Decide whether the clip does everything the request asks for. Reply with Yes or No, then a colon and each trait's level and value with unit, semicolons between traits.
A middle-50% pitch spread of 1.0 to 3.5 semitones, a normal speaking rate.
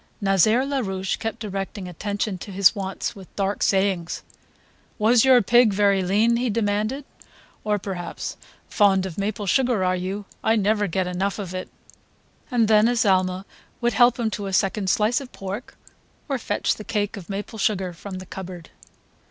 Yes: average, 2.7 semitones; average, 170 wpm